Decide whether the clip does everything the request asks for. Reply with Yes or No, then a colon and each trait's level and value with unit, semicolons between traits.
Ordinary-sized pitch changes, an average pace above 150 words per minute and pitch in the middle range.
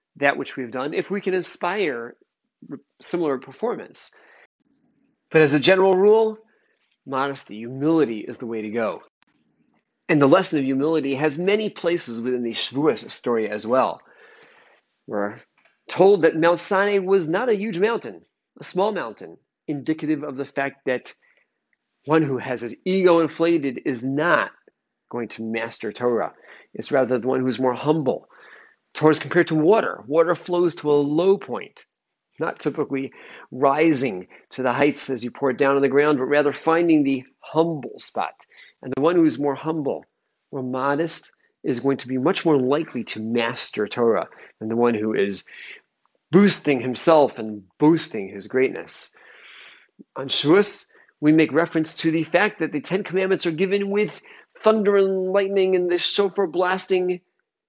No: wide, 5.8 semitones; average, 160 wpm; medium, 150 Hz